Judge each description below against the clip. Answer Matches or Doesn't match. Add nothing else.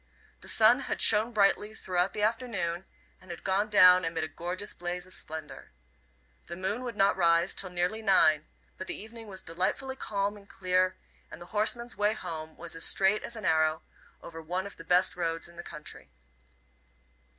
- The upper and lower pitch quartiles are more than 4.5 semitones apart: Doesn't match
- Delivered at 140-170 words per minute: Doesn't match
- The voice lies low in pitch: Doesn't match